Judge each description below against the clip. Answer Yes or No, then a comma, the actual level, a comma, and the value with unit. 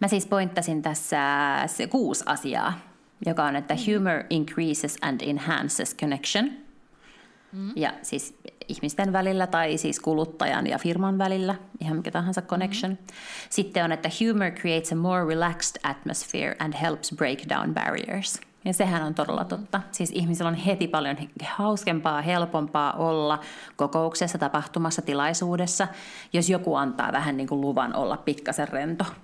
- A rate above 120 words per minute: Yes, average, 140 wpm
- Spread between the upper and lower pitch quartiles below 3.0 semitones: No, average, 3.9 semitones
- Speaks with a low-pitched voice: No, medium, 170 Hz